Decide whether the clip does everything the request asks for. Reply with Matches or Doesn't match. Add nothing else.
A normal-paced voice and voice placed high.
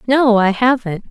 Matches